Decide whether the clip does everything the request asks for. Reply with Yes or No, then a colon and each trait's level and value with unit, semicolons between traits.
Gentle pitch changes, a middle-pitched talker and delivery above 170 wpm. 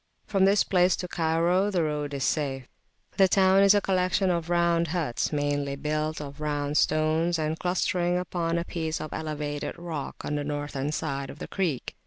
No: average, 3.3 semitones; medium, 160 Hz; average, 185 wpm